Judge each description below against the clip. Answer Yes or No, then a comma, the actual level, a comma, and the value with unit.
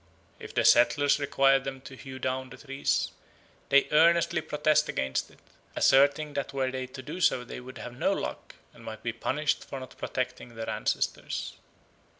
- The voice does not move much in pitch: Yes, narrow, 1.9 semitones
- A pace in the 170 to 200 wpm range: Yes, average, 175 wpm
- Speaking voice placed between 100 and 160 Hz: Yes, low, 135 Hz